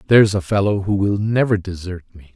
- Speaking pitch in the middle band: No, low, 100 Hz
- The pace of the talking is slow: No, fast, 205 wpm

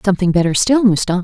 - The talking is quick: No, average, 195 wpm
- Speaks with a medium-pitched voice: No, high, 195 Hz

